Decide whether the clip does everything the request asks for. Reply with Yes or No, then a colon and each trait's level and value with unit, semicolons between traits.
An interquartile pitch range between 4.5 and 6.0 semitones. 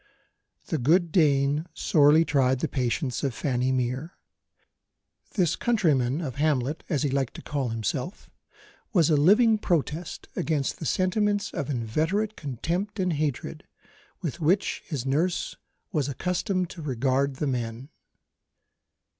Yes: average, 4.9 semitones